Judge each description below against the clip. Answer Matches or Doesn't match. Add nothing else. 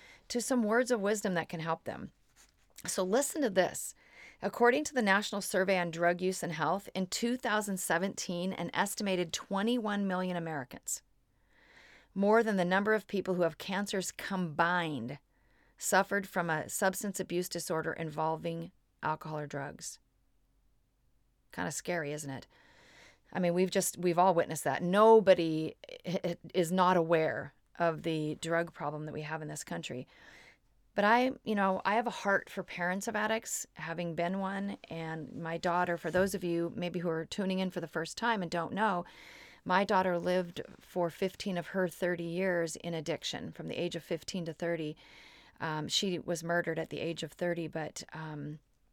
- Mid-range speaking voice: Matches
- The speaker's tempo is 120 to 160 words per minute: Doesn't match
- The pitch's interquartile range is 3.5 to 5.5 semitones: Doesn't match